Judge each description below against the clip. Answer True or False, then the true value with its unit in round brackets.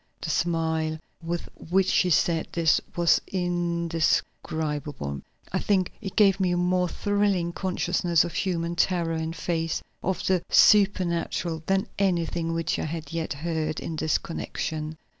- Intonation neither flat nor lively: False (2.1 semitones)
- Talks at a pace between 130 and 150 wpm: True (140 wpm)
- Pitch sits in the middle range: True (170 Hz)